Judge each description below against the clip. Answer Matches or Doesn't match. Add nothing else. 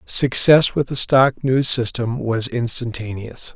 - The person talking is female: Doesn't match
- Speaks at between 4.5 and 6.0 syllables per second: Doesn't match